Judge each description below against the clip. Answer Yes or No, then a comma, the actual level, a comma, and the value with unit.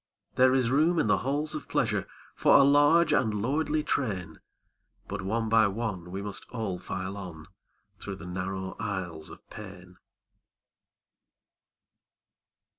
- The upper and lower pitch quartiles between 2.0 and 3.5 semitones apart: No, wide, 5.6 semitones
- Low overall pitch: Yes, low, 105 Hz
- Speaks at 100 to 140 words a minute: Yes, slow, 135 wpm